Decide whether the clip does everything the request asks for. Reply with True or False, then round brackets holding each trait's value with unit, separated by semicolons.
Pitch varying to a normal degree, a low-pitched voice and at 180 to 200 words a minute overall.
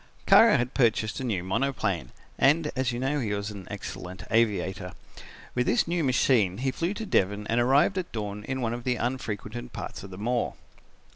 True (4.4 semitones; 120 Hz; 195 wpm)